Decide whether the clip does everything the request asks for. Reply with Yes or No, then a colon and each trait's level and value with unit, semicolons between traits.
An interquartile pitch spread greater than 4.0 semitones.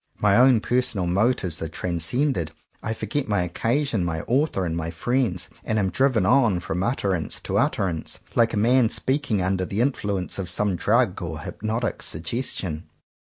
Yes: wide, 5.4 semitones